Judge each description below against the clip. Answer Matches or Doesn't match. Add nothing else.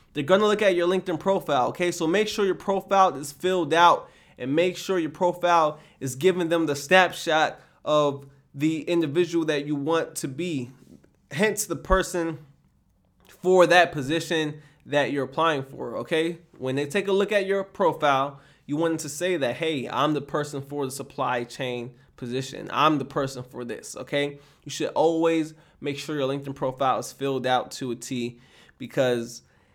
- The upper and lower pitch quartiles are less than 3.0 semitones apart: Doesn't match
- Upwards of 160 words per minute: Matches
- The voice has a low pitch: Doesn't match